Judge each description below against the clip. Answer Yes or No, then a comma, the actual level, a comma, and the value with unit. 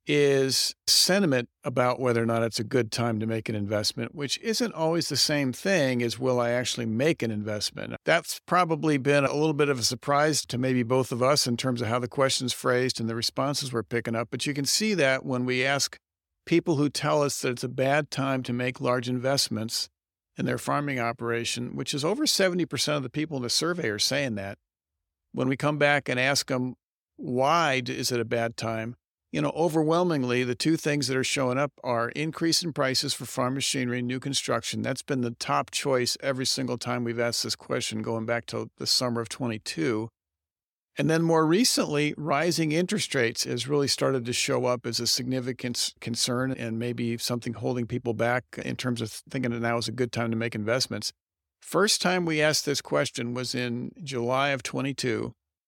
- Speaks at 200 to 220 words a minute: Yes, fast, 205 wpm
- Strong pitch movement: No, average, 3.4 semitones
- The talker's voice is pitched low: Yes, low, 125 Hz